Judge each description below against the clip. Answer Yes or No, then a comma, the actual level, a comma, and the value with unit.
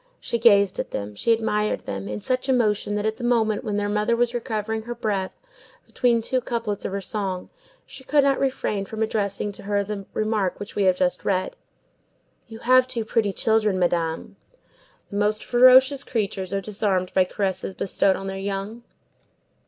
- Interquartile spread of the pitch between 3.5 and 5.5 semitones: No, average, 3.1 semitones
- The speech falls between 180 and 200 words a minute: Yes, average, 185 wpm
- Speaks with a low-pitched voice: No, high, 210 Hz